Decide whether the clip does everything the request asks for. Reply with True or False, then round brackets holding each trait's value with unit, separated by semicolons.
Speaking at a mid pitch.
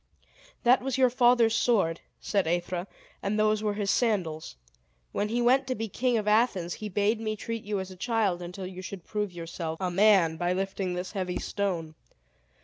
False (200 Hz)